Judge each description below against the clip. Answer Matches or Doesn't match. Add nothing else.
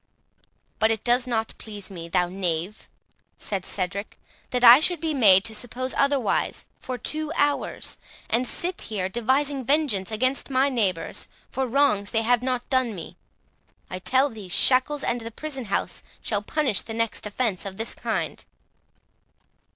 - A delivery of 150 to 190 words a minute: Matches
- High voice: Matches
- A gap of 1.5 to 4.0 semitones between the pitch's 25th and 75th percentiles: Doesn't match